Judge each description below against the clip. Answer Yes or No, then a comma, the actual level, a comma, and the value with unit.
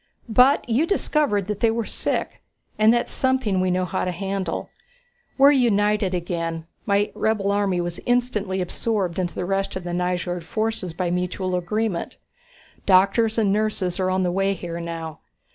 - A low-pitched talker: No, high, 195 Hz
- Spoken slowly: No, average, 165 wpm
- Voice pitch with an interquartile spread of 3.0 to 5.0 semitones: Yes, average, 3.4 semitones